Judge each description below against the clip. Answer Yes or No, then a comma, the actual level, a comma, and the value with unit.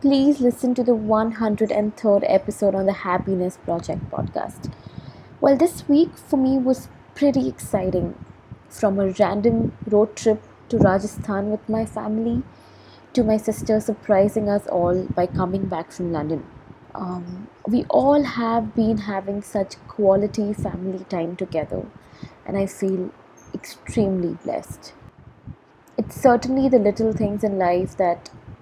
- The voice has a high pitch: Yes, high, 205 Hz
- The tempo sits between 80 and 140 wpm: Yes, slow, 135 wpm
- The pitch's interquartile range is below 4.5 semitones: Yes, average, 3.6 semitones